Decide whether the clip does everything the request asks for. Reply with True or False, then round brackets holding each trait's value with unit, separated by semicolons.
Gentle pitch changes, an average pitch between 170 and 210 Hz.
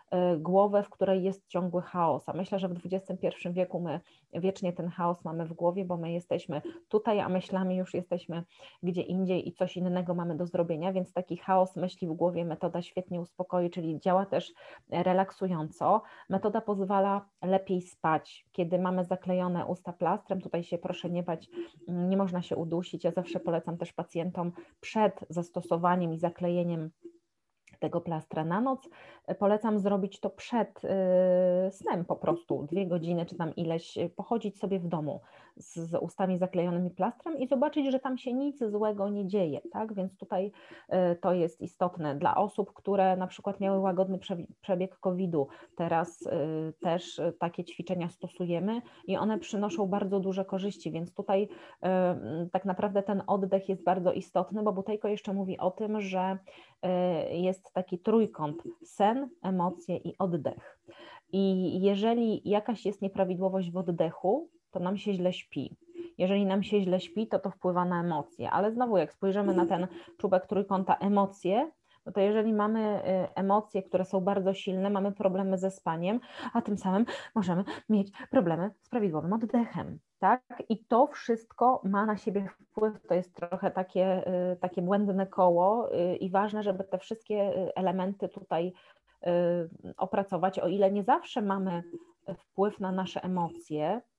True (2.3 semitones; 185 Hz)